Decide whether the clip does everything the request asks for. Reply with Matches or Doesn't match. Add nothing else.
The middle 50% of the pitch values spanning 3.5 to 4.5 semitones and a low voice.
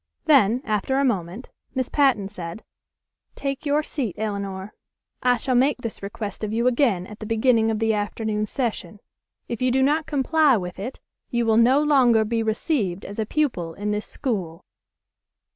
Doesn't match